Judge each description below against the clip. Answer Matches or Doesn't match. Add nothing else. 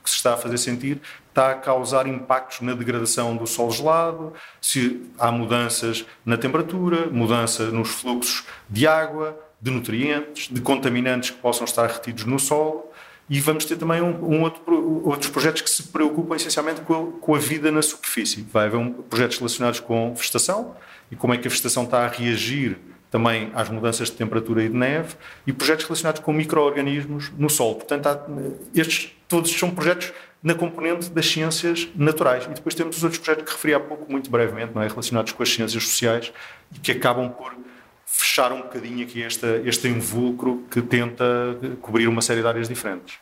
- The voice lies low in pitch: Matches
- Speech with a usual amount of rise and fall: Matches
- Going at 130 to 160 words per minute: Doesn't match